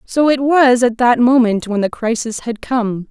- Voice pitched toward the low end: No, high, 240 Hz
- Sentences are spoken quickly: Yes, fast, 210 wpm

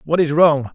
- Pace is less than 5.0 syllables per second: Yes, 4.7 syllables/s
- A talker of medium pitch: Yes, medium, 155 Hz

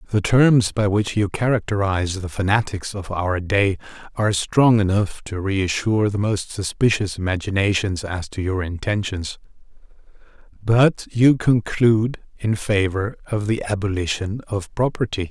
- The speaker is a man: Yes, male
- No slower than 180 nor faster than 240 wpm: No, slow, 135 wpm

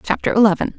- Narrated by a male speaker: No, female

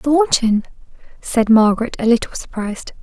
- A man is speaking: No, female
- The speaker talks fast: No, slow, 120 wpm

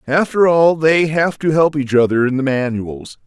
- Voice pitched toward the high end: No, medium, 145 Hz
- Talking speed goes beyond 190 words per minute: Yes, average, 200 wpm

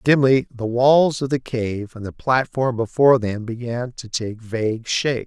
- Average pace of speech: Yes, average, 180 wpm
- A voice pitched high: No, low, 120 Hz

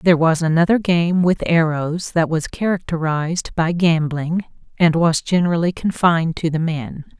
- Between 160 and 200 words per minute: No, average, 150 wpm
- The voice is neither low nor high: Yes, medium, 165 Hz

